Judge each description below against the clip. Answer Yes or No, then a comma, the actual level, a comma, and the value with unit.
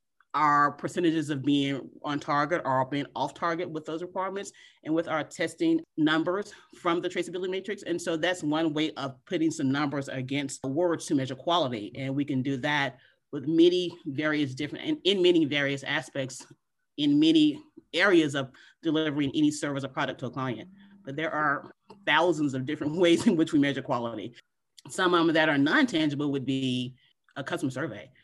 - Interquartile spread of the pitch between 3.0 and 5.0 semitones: Yes, average, 3.9 semitones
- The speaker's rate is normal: Yes, average, 185 wpm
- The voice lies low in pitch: No, medium, 155 Hz